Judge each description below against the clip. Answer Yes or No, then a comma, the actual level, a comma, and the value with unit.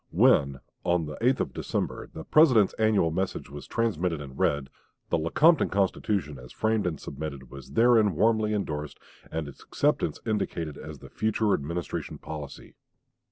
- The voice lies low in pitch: Yes, very low, 85 Hz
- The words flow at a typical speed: Yes, average, 155 wpm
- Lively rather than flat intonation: Yes, wide, 6.8 semitones